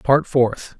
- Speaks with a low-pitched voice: Yes, low, 130 Hz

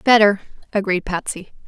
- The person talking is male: No, female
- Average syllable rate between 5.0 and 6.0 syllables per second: Yes, 5.2 syllables/s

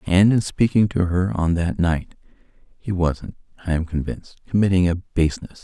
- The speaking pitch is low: Yes, very low, 90 Hz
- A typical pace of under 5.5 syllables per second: Yes, 5.2 syllables/s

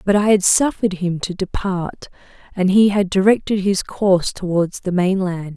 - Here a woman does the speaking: Yes, female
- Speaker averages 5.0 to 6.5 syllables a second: No, 4.8 syllables/s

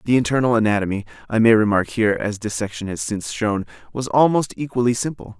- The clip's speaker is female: No, male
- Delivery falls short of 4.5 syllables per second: No, 6.4 syllables/s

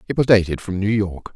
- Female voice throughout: No, male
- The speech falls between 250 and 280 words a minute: Yes, fast, 265 wpm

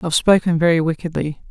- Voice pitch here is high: No, medium, 165 Hz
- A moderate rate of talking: Yes, average, 160 wpm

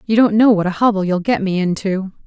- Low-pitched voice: No, high, 200 Hz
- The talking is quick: Yes, fast, 265 wpm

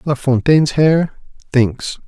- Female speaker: No, male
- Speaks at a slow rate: Yes, slow, 115 wpm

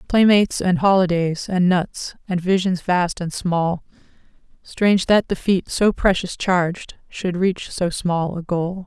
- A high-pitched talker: No, medium, 180 Hz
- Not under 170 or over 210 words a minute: No, average, 155 wpm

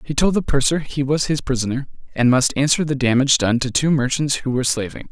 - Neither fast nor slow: No, fast, 235 wpm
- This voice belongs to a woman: No, male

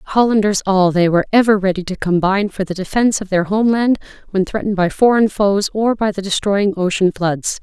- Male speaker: No, female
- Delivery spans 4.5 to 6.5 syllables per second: Yes, 5.8 syllables/s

